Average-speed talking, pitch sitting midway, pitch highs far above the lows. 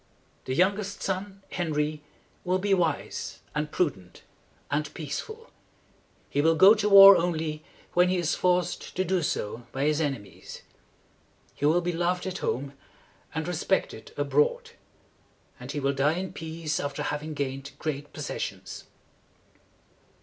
No: average, 150 wpm; medium, 165 Hz; average, 4.1 semitones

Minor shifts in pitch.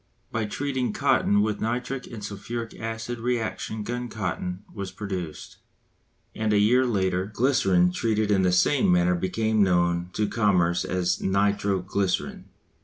No: average, 3.5 semitones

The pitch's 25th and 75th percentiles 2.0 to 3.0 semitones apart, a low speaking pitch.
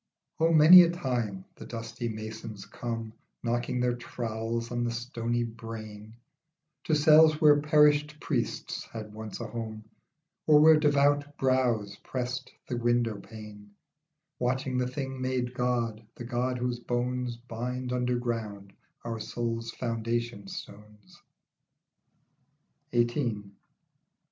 Yes: narrow, 2.4 semitones; low, 120 Hz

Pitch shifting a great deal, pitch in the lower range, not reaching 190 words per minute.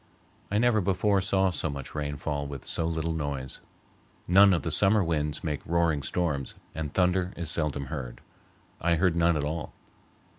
No: average, 3.7 semitones; very low, 80 Hz; average, 175 wpm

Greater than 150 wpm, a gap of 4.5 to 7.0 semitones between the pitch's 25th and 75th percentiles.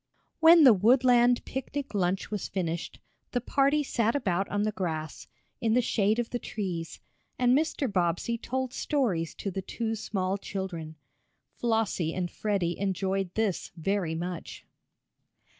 No: average, 140 wpm; average, 5.0 semitones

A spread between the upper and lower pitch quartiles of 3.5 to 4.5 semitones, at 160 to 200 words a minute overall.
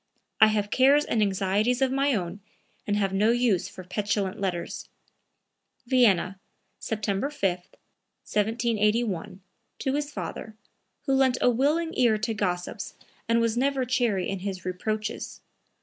No: average, 4.2 semitones; slow, 135 wpm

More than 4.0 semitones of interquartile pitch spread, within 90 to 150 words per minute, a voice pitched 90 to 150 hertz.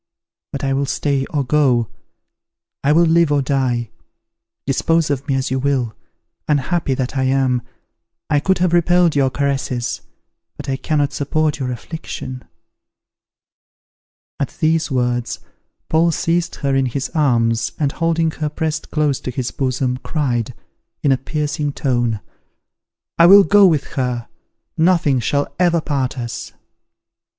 No: average, 3.5 semitones; average, 140 wpm; medium, 140 Hz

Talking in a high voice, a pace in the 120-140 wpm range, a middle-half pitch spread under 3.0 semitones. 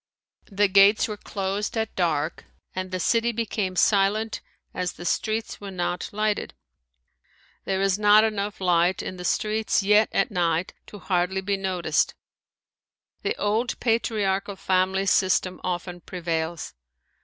Yes: high, 195 Hz; slow, 135 wpm; narrow, 2.6 semitones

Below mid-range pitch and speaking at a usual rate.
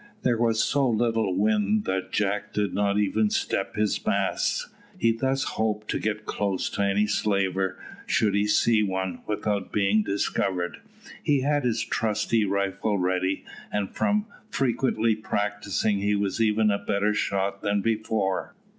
Yes: low, 105 Hz; average, 150 wpm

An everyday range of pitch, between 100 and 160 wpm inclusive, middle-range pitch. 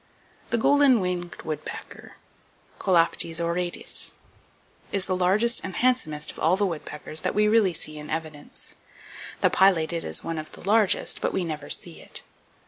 Yes: average, 4.1 semitones; average, 155 wpm; medium, 175 Hz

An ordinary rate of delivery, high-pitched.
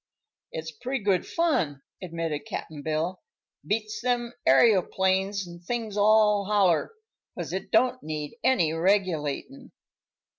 No: slow, 115 wpm; high, 195 Hz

